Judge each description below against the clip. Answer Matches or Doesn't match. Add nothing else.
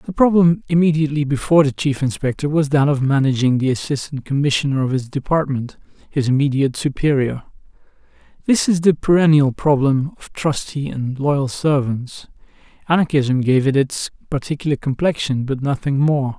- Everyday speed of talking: Matches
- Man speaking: Matches